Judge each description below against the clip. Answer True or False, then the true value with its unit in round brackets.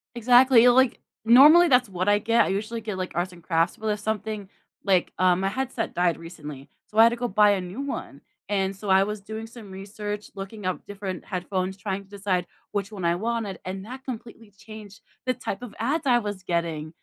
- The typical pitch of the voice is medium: False (205 Hz)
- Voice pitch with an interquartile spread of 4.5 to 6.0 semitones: False (3.5 semitones)